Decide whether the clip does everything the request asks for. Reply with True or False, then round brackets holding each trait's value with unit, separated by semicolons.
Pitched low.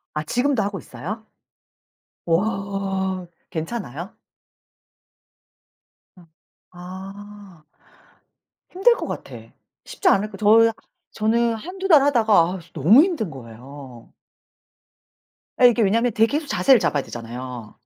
False (200 Hz)